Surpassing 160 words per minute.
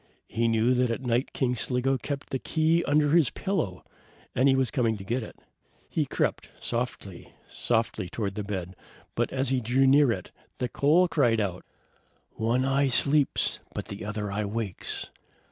Yes: average, 175 wpm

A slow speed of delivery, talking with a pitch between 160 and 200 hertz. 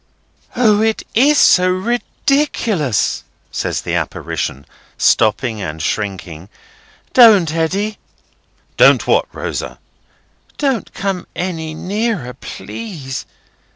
Yes: slow, 90 wpm; medium, 185 Hz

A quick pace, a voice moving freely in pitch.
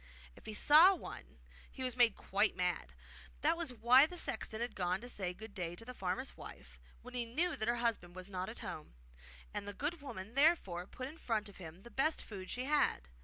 Yes: fast, 220 wpm; wide, 6.1 semitones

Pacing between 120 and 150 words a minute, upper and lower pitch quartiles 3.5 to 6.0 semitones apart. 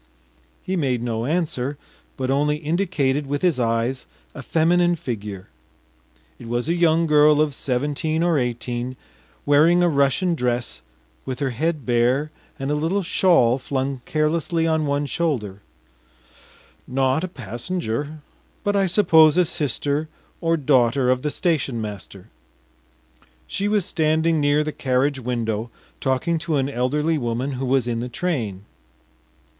Yes: average, 140 wpm; average, 4.6 semitones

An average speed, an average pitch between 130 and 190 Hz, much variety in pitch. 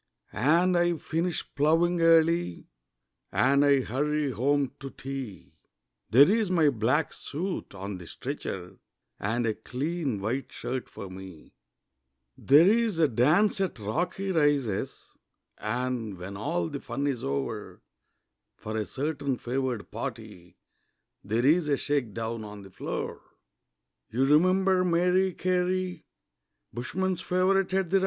No: slow, 125 wpm; medium, 140 Hz; wide, 7.3 semitones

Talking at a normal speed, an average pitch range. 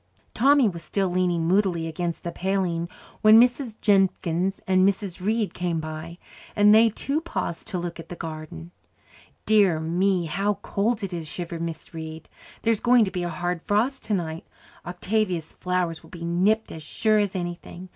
Yes: average, 170 wpm; average, 3.6 semitones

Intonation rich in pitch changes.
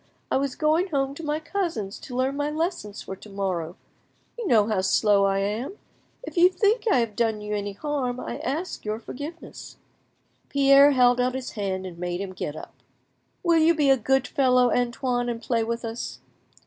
Yes: wide, 5.9 semitones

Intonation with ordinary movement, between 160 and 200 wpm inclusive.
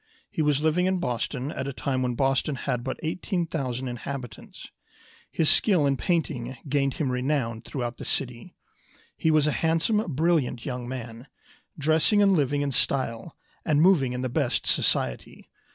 Yes: average, 4.0 semitones; average, 165 wpm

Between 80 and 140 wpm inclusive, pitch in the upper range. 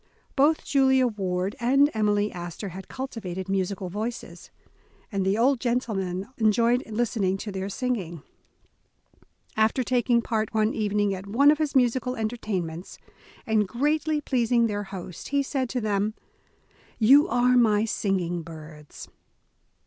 Yes: slow, 135 wpm; high, 220 Hz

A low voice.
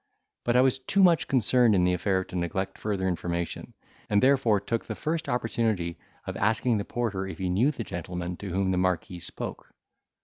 Yes: low, 100 Hz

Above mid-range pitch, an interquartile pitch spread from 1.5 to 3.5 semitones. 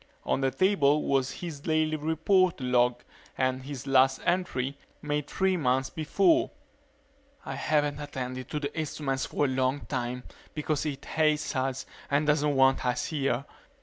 No: medium, 140 Hz; average, 2.9 semitones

